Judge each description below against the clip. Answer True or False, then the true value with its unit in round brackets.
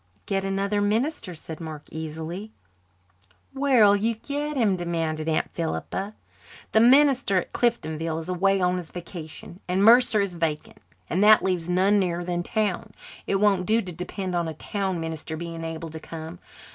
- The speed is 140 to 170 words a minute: True (165 wpm)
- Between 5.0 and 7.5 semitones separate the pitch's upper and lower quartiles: False (4.1 semitones)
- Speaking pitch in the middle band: True (180 Hz)